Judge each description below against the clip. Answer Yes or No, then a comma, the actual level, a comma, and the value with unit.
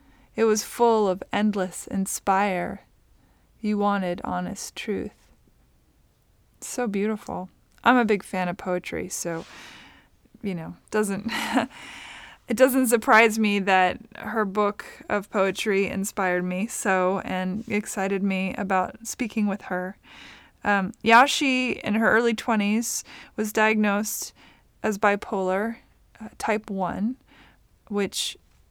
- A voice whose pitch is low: No, high, 205 Hz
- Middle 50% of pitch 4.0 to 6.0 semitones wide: No, average, 2.8 semitones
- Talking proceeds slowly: Yes, slow, 115 wpm